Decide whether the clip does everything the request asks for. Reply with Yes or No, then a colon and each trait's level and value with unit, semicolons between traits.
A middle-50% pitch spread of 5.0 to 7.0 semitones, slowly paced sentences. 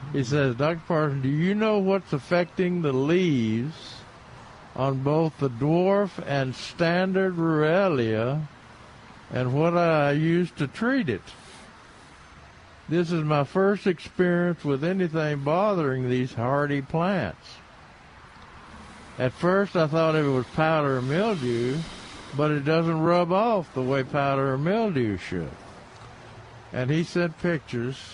Yes: average, 5.3 semitones; slow, 130 wpm